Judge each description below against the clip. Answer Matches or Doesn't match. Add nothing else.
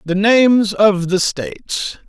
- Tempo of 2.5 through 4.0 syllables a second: Matches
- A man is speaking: Matches